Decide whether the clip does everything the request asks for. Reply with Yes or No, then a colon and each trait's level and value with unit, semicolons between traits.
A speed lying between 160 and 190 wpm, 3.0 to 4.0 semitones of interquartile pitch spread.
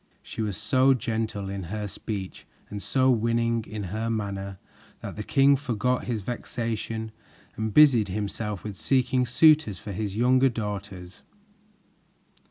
No: average, 140 wpm; average, 3.5 semitones